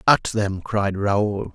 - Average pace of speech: Yes, average, 155 wpm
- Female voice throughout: No, male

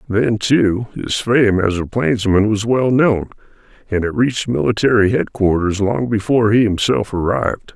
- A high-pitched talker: No, low, 105 Hz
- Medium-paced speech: Yes, average, 155 wpm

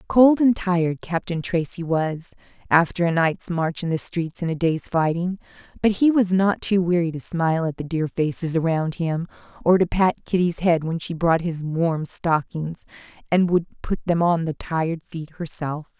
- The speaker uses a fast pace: No, average, 190 wpm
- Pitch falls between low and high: Yes, medium, 170 Hz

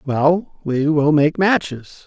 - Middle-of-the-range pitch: Yes, medium, 155 Hz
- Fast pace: No, average, 145 wpm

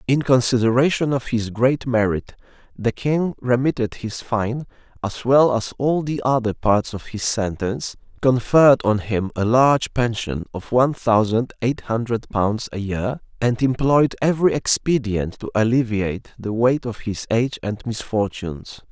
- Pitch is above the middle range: No, low, 120 Hz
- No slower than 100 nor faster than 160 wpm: Yes, average, 150 wpm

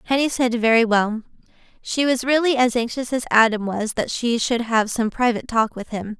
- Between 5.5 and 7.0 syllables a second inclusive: No, 5.3 syllables/s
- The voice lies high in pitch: Yes, high, 235 Hz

